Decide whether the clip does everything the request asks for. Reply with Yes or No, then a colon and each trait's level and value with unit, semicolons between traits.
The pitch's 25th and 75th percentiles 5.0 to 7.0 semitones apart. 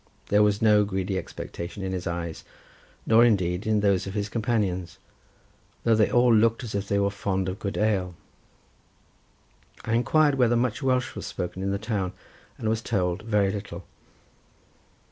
No: average, 3.0 semitones